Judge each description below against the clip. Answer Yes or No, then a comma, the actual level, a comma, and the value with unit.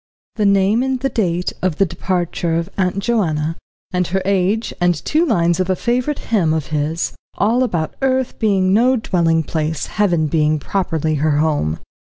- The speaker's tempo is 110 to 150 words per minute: No, average, 170 wpm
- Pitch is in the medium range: Yes, medium, 180 Hz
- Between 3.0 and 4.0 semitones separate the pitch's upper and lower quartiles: No, average, 5.0 semitones